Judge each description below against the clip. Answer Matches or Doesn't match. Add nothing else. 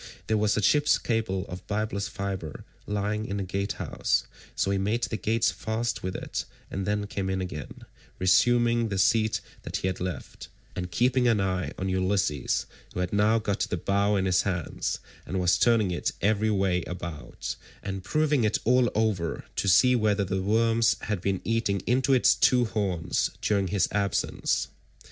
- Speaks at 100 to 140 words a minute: Doesn't match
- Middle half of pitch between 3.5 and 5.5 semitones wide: Doesn't match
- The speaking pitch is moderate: Doesn't match